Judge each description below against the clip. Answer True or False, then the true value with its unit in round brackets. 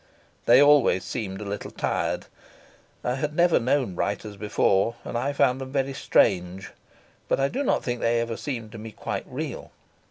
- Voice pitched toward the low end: True (120 Hz)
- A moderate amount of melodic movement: True (4.8 semitones)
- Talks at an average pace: True (180 wpm)